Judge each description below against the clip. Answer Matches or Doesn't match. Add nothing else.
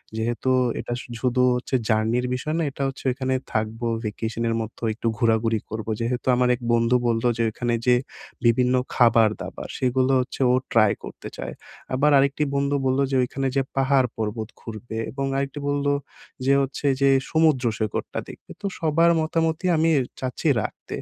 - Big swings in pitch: Doesn't match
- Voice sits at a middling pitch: Doesn't match